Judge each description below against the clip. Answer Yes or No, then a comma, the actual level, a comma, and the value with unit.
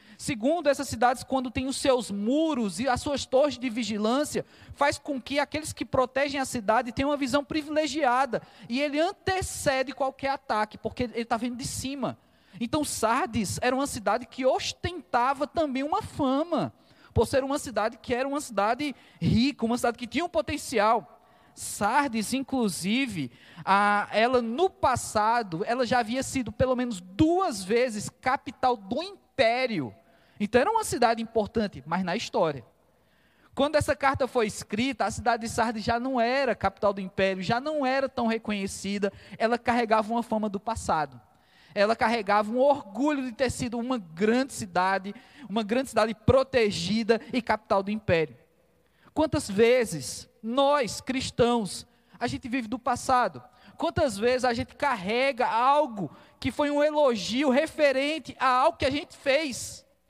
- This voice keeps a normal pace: Yes, average, 155 wpm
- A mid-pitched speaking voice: No, very high, 250 Hz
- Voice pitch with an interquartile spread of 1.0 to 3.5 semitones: No, average, 4.0 semitones